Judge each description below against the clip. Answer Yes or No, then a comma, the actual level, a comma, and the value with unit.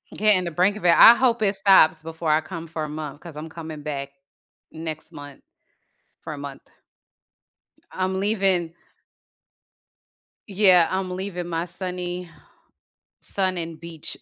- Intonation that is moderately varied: Yes, average, 3.1 semitones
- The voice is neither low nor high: Yes, medium, 170 Hz